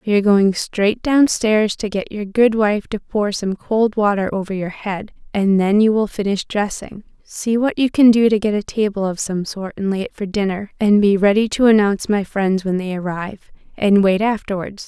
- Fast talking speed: Yes, fast, 215 wpm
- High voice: Yes, high, 205 Hz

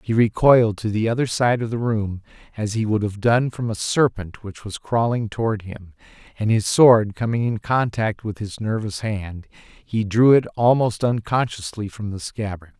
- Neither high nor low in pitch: No, low, 110 Hz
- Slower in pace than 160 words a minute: No, average, 190 wpm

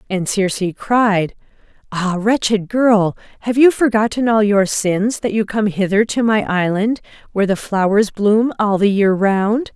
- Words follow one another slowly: No, average, 165 wpm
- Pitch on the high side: Yes, high, 210 Hz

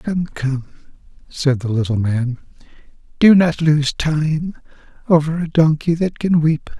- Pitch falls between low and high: Yes, medium, 155 Hz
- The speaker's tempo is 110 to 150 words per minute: Yes, average, 140 wpm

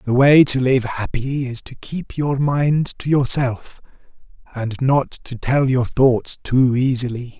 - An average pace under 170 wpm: Yes, average, 160 wpm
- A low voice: Yes, low, 130 Hz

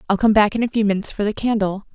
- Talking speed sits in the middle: No, fast, 310 wpm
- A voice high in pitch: Yes, high, 210 Hz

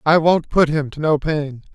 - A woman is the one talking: No, male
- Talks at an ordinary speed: No, fast, 240 wpm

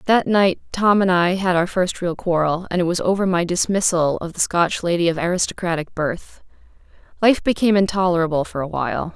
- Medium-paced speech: Yes, average, 190 wpm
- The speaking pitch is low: No, medium, 180 Hz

